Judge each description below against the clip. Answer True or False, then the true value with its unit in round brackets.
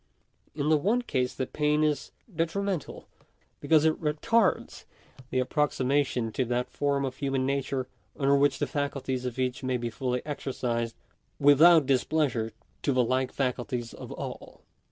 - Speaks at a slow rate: False (155 wpm)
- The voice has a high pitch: False (135 Hz)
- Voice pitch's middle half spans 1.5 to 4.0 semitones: True (2.9 semitones)